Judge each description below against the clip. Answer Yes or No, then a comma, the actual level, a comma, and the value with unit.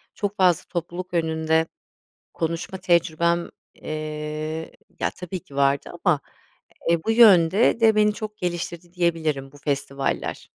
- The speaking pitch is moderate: Yes, medium, 170 Hz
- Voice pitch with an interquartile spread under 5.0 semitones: Yes, average, 2.9 semitones